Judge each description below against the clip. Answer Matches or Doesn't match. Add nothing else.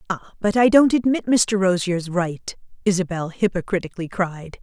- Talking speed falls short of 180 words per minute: Matches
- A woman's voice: Matches